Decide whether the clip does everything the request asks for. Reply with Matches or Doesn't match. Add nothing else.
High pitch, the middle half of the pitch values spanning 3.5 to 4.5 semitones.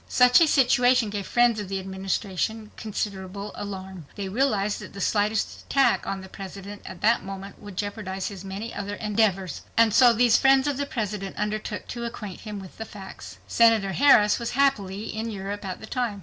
Doesn't match